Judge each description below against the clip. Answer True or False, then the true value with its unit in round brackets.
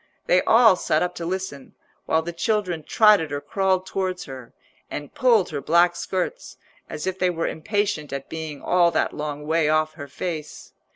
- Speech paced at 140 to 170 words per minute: False (180 wpm)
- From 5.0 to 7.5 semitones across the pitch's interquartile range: False (3.6 semitones)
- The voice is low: False (170 Hz)